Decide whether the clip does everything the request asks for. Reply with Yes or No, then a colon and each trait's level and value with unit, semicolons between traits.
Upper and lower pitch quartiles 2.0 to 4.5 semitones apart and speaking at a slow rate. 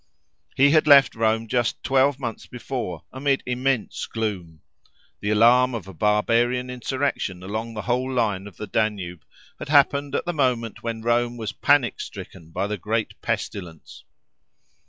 No: average, 3.7 semitones; average, 155 wpm